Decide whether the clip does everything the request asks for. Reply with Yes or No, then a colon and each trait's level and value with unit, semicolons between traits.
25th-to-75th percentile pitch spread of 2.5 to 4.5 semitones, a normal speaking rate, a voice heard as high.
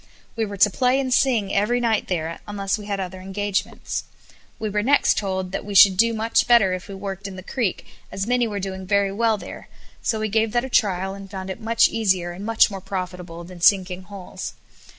No: average, 2.8 semitones; fast, 220 wpm; high, 200 Hz